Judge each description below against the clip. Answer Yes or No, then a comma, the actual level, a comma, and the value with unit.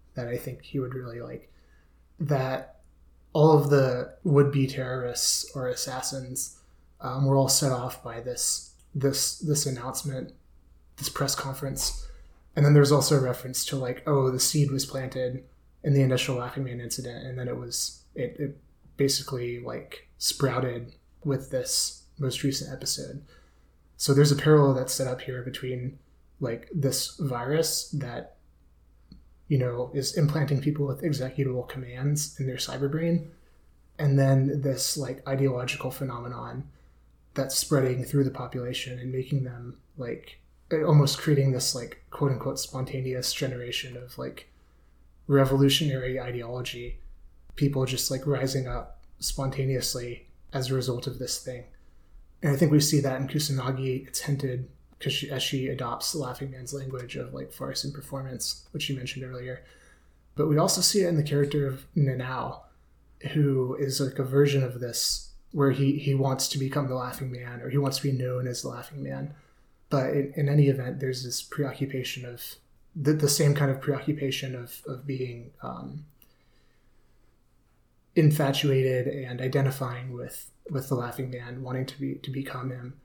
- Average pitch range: No, narrow, 2.1 semitones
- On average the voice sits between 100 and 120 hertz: No, low, 130 Hz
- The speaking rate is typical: Yes, average, 160 wpm